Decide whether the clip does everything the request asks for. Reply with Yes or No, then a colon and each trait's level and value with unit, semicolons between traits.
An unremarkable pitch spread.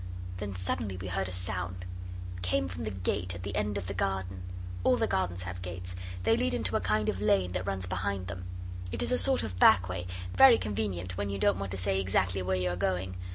No: narrow, 1.5 semitones